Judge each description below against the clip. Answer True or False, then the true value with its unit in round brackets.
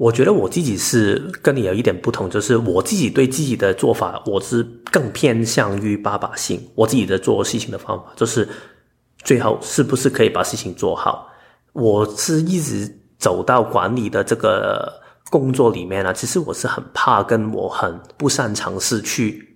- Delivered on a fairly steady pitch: False (4.3 semitones)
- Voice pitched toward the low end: True (115 Hz)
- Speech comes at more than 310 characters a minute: False (270 characters per minute)